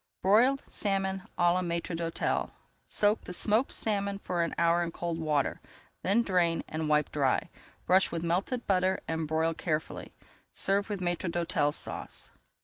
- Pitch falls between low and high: Yes, medium, 175 Hz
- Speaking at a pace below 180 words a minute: Yes, average, 155 wpm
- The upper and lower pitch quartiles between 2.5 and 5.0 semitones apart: Yes, average, 3.1 semitones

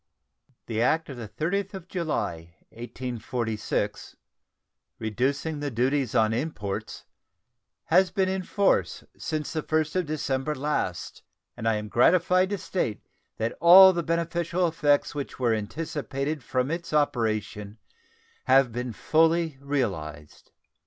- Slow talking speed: Yes, slow, 125 wpm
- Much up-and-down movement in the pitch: Yes, wide, 6.3 semitones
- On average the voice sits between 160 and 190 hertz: No, medium, 145 Hz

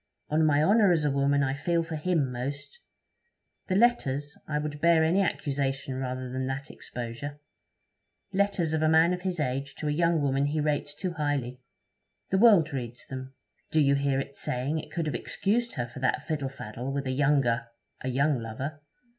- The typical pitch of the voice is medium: Yes, medium, 145 Hz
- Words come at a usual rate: Yes, average, 190 wpm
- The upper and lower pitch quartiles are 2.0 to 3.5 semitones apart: Yes, average, 3.2 semitones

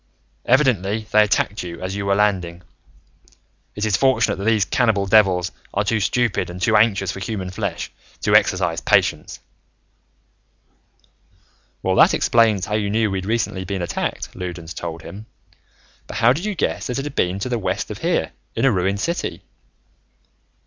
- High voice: No, low, 100 Hz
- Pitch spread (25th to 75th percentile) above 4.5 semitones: No, average, 3.4 semitones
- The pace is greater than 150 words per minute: Yes, average, 170 wpm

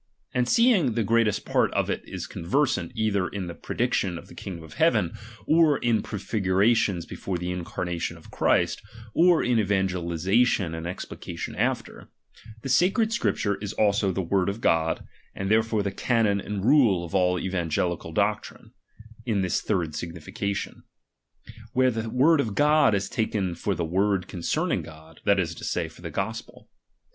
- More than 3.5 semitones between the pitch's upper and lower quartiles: Yes, average, 4.5 semitones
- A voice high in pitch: No, low, 100 Hz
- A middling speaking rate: Yes, average, 165 wpm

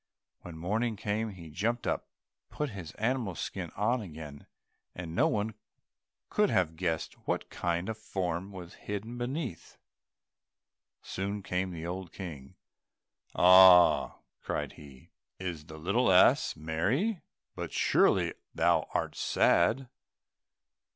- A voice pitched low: Yes, very low, 95 Hz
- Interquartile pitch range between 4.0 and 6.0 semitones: Yes, average, 4.7 semitones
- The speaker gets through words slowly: Yes, slow, 130 wpm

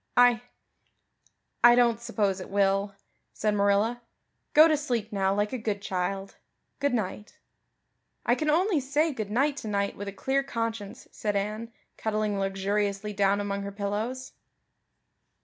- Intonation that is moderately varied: Yes, average, 3.4 semitones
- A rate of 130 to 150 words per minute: Yes, average, 145 wpm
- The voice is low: No, high, 210 Hz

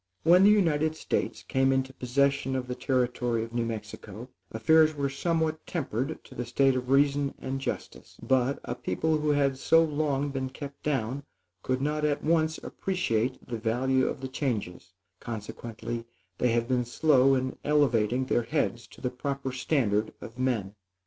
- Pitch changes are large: No, average, 3.3 semitones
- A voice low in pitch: Yes, low, 130 Hz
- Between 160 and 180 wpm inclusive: Yes, average, 170 wpm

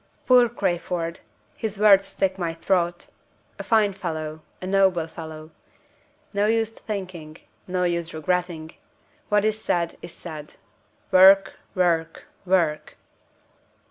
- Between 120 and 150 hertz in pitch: No, medium, 180 Hz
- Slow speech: Yes, slow, 120 wpm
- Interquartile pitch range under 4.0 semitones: Yes, average, 3.2 semitones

